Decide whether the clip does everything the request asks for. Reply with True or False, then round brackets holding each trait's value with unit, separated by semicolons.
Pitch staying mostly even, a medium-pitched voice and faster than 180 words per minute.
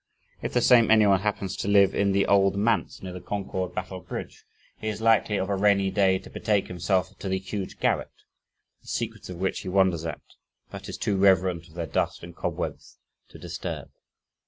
False (1.8 semitones; 95 Hz; 200 wpm)